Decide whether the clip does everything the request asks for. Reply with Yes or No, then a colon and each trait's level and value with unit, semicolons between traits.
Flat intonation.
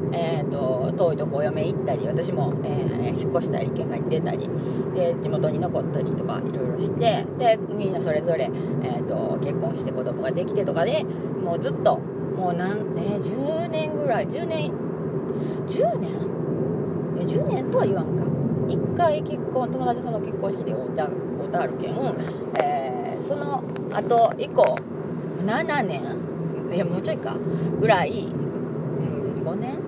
Yes: narrow, 1.2 semitones